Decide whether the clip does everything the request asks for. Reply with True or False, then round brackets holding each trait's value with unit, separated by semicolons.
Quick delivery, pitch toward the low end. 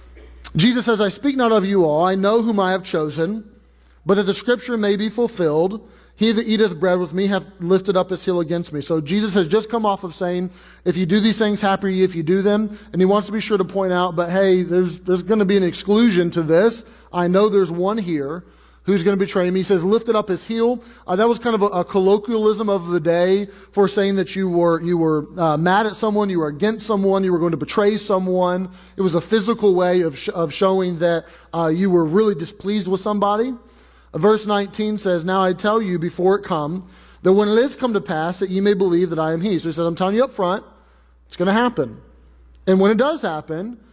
False (245 wpm; 190 Hz)